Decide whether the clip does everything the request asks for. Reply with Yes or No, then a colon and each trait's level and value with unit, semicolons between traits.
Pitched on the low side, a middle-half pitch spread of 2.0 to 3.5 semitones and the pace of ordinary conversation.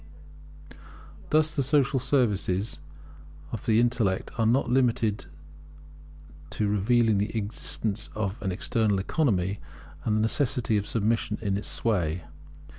No: low, 110 Hz; average, 3.2 semitones; slow, 120 wpm